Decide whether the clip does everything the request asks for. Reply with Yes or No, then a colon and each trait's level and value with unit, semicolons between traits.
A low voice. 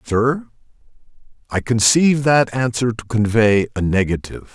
Yes: low, 115 Hz